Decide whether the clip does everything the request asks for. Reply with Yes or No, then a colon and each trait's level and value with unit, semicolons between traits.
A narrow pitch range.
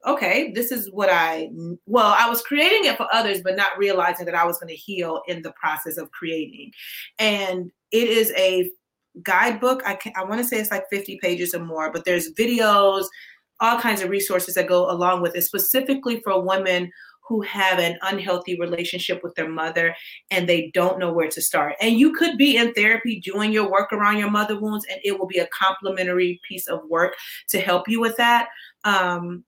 No: average, 3.3 semitones